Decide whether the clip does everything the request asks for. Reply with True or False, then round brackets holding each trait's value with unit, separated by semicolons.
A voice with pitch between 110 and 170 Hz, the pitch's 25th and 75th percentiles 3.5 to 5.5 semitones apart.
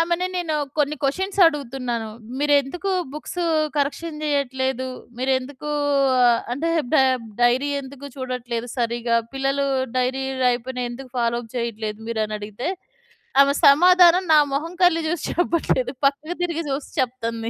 False (270 Hz; 4.2 semitones)